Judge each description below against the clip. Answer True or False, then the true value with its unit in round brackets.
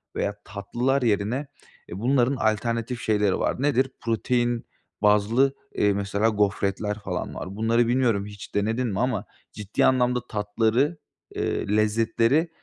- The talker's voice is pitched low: True (115 Hz)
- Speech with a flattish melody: False (3.2 semitones)